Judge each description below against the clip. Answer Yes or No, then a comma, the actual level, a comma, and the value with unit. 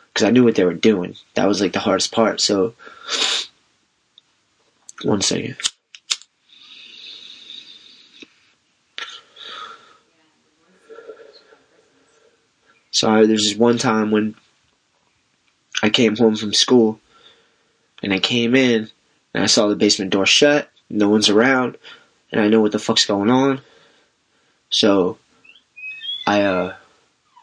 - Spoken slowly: Yes, slow, 115 wpm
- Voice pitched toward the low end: Yes, low, 115 Hz